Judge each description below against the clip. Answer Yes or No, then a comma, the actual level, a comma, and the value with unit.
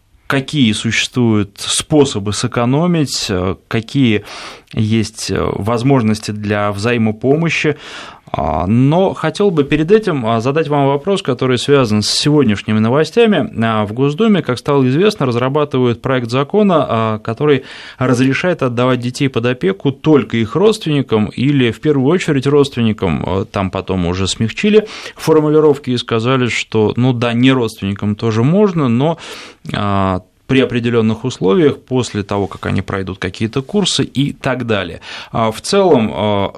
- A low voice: Yes, low, 125 Hz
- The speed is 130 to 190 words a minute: No, average, 120 wpm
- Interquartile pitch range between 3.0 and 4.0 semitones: No, average, 5.0 semitones